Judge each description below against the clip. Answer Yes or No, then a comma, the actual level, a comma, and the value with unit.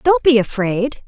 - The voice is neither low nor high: No, very high, 255 Hz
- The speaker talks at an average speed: Yes, average, 170 wpm